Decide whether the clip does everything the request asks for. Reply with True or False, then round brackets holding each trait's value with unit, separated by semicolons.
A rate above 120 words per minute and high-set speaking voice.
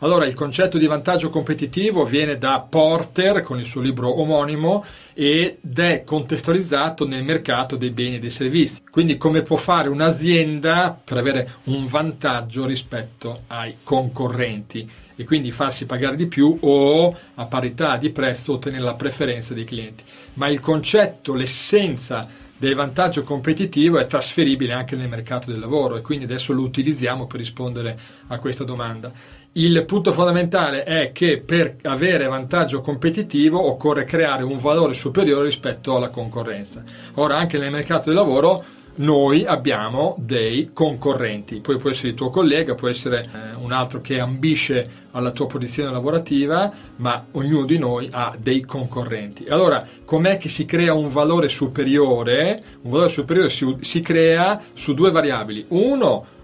False (155 wpm; 140 Hz)